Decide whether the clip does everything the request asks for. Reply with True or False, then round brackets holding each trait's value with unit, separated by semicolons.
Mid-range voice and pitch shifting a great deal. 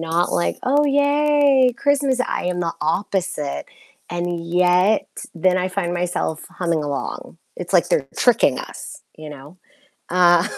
True (180 Hz; 6.8 semitones)